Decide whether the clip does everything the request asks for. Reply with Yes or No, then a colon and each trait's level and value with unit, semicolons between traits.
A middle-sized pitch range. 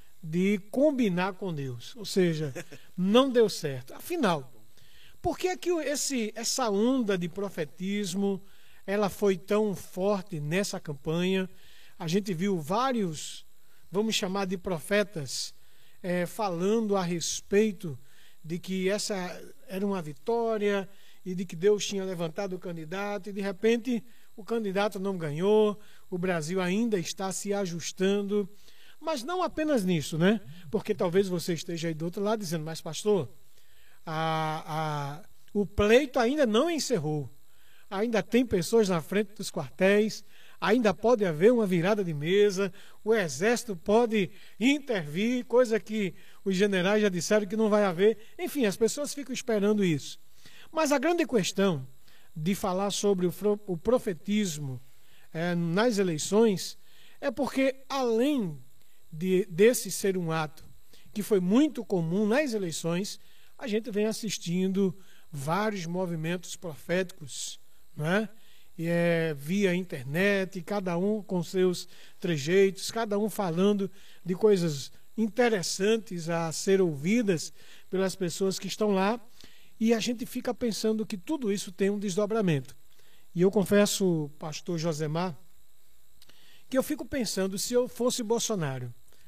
Yes: average, 3.8 semitones